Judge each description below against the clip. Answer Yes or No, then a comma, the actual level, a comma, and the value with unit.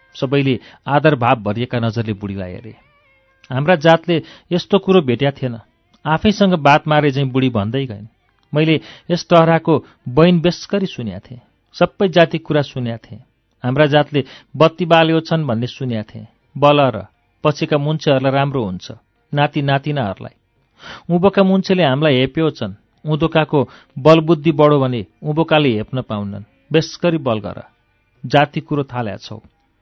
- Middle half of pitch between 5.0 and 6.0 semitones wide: Yes, wide, 5.5 semitones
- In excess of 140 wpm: No, slow, 135 wpm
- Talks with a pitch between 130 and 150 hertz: Yes, medium, 140 Hz